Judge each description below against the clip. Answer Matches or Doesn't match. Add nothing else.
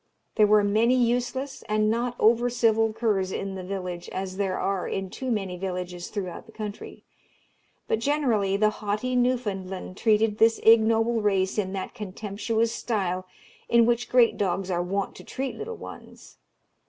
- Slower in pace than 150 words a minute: Doesn't match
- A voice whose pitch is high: Matches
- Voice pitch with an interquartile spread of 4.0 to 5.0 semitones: Doesn't match